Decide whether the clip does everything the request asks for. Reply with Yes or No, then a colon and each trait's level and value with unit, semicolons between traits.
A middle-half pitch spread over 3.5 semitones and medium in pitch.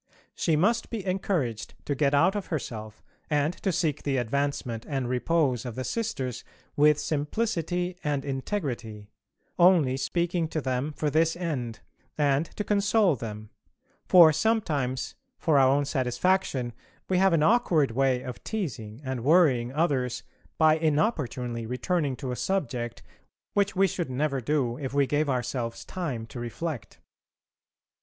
Yes: wide, 5.4 semitones; medium, 145 Hz